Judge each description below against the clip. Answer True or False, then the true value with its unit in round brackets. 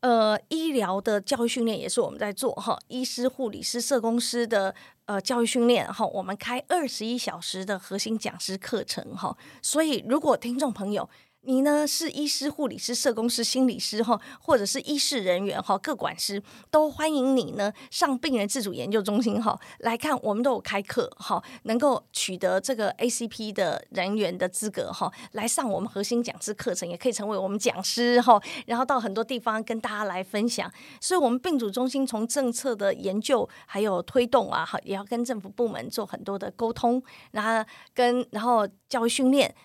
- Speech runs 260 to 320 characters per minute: True (295 characters per minute)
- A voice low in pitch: False (235 Hz)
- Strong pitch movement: False (4.1 semitones)